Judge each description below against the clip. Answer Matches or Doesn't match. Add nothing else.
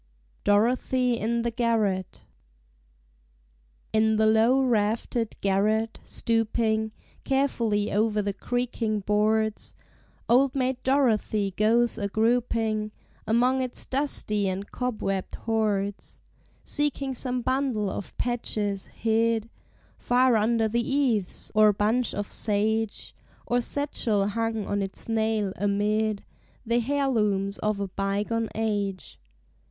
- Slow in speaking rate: Matches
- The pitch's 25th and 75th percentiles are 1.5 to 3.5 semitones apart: Matches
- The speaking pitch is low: Doesn't match